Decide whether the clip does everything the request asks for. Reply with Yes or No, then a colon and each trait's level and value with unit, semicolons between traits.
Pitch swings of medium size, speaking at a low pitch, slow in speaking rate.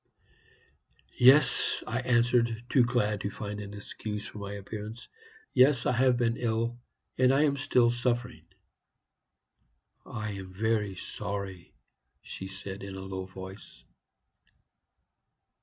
Yes: average, 3.5 semitones; low, 110 Hz; slow, 125 wpm